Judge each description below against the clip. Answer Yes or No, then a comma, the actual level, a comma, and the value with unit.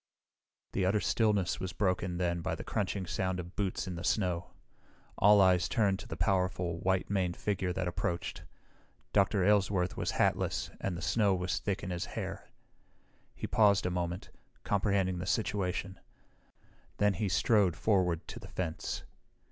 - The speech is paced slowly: No, average, 160 wpm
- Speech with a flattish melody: Yes, narrow, 2.1 semitones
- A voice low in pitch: Yes, very low, 95 Hz